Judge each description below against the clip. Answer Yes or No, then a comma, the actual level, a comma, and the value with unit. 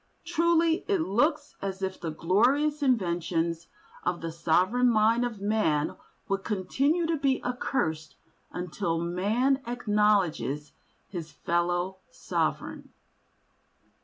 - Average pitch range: No, wide, 7.3 semitones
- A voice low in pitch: No, high, 200 Hz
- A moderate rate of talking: No, slow, 105 wpm